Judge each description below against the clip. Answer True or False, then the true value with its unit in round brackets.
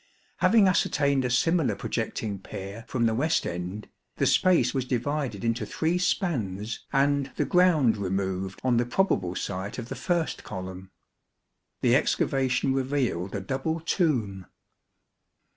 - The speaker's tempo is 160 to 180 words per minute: False (135 wpm)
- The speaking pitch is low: True (125 Hz)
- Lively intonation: True (7.0 semitones)